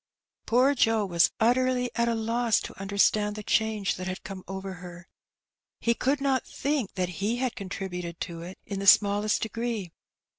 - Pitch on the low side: No, high, 210 Hz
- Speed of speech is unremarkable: Yes, average, 175 wpm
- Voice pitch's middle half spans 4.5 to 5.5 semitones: No, average, 3.9 semitones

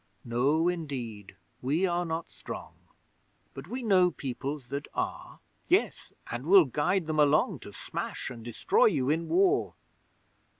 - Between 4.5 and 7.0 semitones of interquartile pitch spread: Yes, wide, 5.5 semitones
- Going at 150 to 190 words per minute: No, average, 140 wpm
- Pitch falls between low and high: Yes, medium, 155 Hz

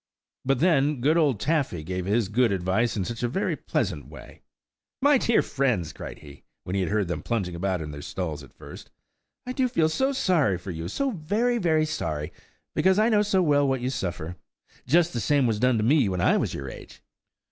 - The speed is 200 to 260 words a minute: Yes, fast, 205 wpm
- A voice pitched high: No, low, 125 Hz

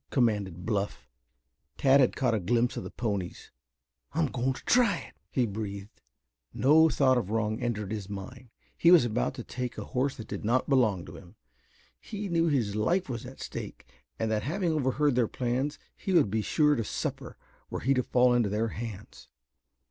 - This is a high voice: No, low, 120 Hz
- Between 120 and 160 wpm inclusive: No, average, 190 wpm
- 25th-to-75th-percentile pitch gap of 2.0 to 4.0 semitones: No, average, 4.5 semitones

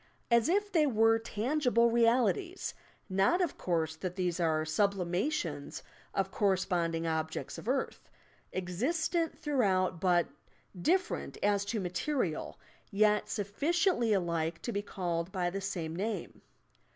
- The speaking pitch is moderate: No, high, 200 Hz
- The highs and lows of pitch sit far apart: Yes, wide, 5.8 semitones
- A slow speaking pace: Yes, slow, 125 wpm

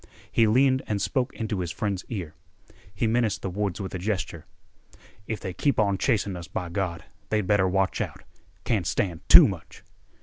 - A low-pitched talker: Yes, low, 100 Hz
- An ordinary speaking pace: Yes, average, 180 wpm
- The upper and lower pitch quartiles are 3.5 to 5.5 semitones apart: No, average, 3.1 semitones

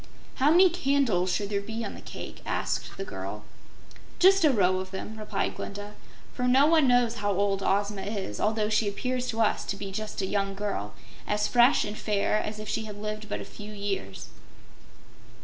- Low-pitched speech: No, high, 210 Hz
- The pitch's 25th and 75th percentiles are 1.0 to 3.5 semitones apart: Yes, average, 3.2 semitones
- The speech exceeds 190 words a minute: Yes, average, 200 wpm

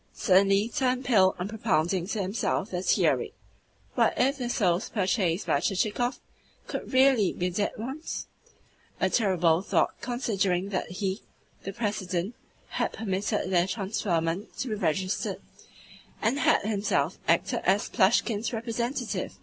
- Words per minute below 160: Yes, slow, 135 wpm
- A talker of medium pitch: No, high, 200 Hz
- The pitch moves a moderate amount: Yes, average, 3.9 semitones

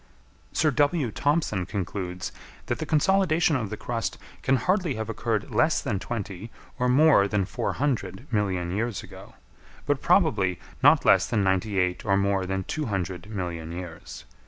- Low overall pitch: Yes, low, 105 Hz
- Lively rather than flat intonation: Yes, wide, 6.7 semitones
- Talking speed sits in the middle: Yes, average, 160 wpm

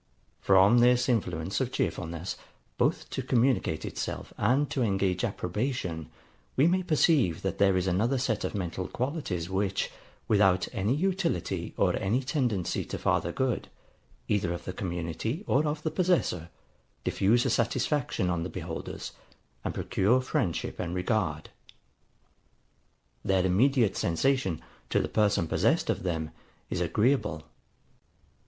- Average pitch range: No, wide, 6.3 semitones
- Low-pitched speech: Yes, low, 105 Hz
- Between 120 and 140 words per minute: Yes, slow, 135 wpm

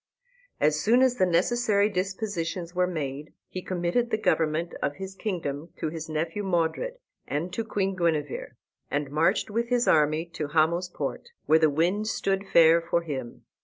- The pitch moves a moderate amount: Yes, average, 4.0 semitones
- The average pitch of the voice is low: No, medium, 170 Hz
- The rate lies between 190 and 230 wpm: No, average, 165 wpm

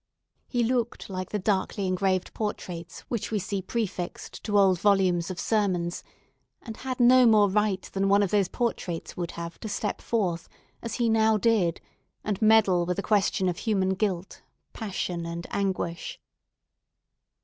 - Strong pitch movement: No, average, 3.3 semitones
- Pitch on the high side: Yes, high, 195 Hz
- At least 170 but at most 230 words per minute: No, average, 160 wpm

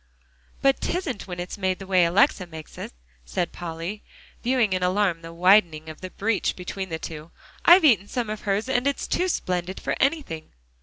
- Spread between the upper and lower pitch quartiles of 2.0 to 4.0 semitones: No, average, 5.0 semitones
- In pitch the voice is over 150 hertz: Yes, high, 190 Hz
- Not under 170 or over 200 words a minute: Yes, average, 190 wpm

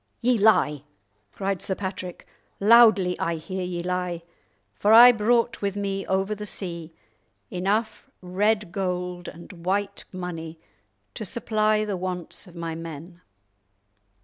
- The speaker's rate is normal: No, slow, 130 wpm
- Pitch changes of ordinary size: Yes, average, 3.0 semitones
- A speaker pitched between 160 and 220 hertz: Yes, high, 190 Hz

